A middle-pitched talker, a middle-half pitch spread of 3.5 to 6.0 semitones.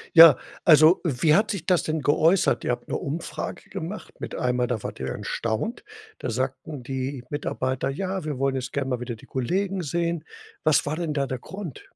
Yes: medium, 150 Hz; average, 4.5 semitones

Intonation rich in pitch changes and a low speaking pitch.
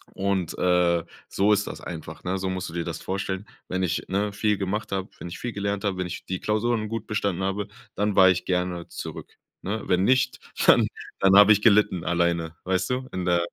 No: narrow, 2.4 semitones; very low, 95 Hz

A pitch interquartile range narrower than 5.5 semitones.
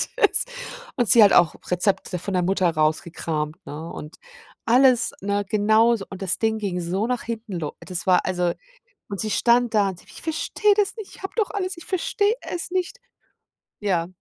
No: wide, 5.8 semitones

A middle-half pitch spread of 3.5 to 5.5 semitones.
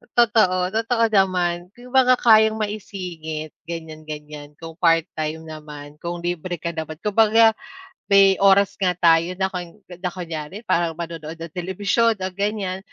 Yes: average, 3.8 semitones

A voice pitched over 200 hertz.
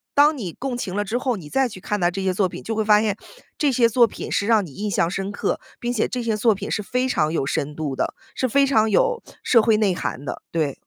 Yes: high, 215 Hz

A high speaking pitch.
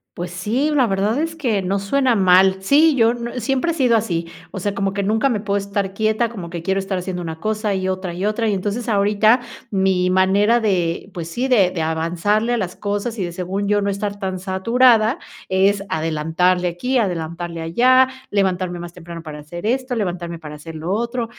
Yes: high, 195 Hz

